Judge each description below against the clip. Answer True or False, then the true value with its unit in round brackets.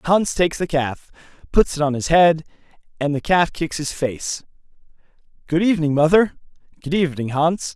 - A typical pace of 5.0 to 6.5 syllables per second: True (5.1 syllables/s)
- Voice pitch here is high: False (155 Hz)